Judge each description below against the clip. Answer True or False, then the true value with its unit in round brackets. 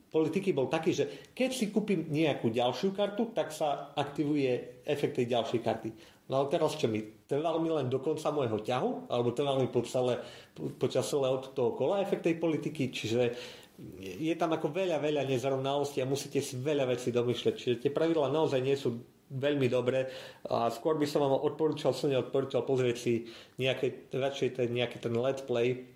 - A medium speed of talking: False (180 wpm)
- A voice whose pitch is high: False (135 Hz)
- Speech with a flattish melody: False (4.2 semitones)